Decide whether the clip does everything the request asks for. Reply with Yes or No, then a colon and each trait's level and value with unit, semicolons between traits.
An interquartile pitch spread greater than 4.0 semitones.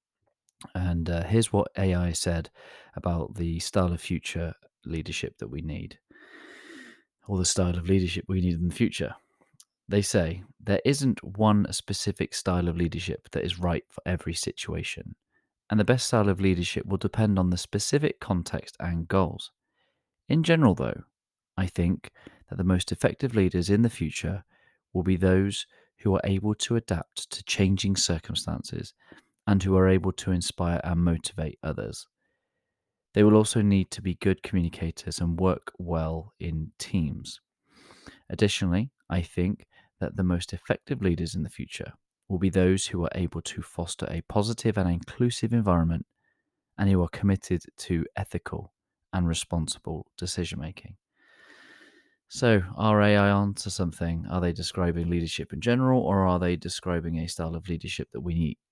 No: average, 3.1 semitones